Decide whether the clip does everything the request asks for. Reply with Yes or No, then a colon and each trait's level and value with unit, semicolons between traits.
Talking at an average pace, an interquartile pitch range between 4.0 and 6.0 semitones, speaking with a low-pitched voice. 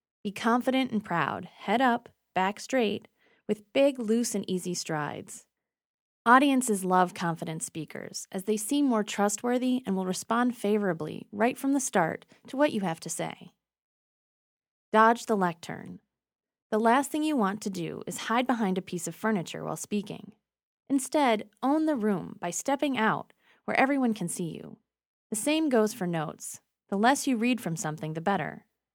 No: average, 170 wpm; average, 5.0 semitones; high, 215 Hz